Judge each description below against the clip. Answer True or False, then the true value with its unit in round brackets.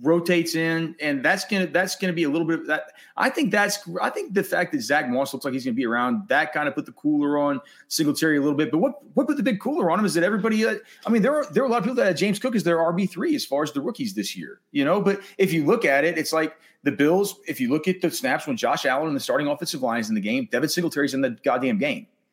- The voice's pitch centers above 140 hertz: True (185 Hz)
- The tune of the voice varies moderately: False (6.8 semitones)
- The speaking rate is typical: False (310 wpm)